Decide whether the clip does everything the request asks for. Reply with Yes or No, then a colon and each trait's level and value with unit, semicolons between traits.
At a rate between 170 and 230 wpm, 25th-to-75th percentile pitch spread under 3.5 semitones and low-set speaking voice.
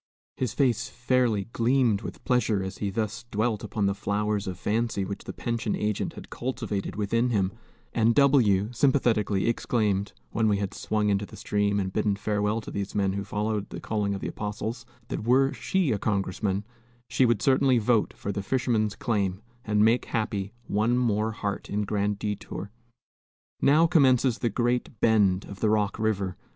Yes: average, 175 wpm; average, 2.8 semitones; low, 105 Hz